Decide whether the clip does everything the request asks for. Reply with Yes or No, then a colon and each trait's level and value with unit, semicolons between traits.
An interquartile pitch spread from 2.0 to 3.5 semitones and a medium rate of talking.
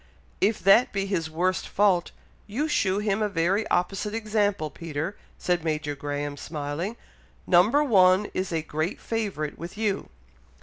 No: average, 4.5 semitones; average, 145 wpm